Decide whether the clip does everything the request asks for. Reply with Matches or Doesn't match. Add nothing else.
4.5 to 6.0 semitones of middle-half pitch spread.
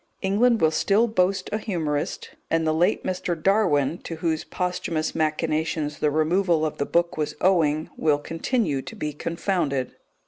Doesn't match